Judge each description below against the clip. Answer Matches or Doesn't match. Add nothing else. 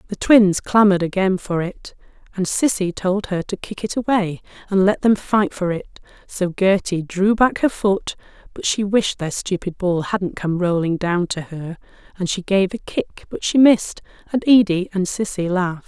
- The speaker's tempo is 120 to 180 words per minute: Doesn't match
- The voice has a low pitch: Doesn't match